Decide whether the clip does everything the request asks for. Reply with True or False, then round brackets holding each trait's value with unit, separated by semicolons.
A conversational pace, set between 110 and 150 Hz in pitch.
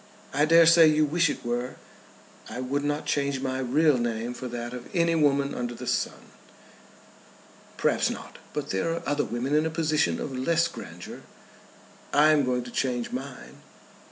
True (175 wpm; 140 Hz)